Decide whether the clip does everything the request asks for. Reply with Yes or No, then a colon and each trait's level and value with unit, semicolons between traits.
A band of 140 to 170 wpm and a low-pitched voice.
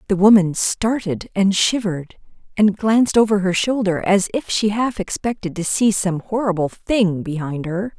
No: average, 165 wpm; high, 200 Hz